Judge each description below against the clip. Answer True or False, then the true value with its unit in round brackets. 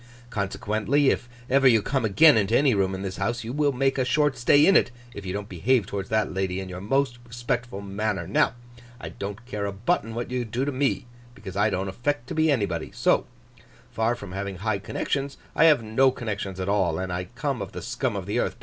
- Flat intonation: False (5.0 semitones)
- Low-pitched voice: True (110 Hz)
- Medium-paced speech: False (230 wpm)